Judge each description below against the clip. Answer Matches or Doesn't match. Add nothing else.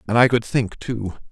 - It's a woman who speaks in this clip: Doesn't match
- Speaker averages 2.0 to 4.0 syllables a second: Doesn't match